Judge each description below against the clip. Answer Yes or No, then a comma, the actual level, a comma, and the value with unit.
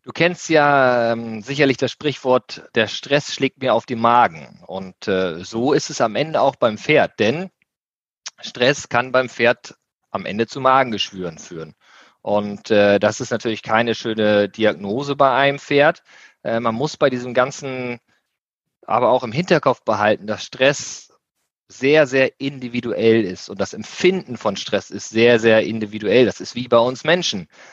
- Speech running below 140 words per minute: No, average, 165 wpm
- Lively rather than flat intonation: No, average, 4.0 semitones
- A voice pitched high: No, low, 125 Hz